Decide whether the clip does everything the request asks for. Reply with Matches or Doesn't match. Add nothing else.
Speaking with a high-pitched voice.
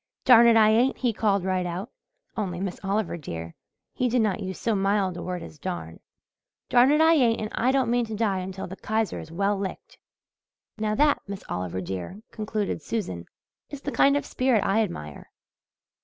Matches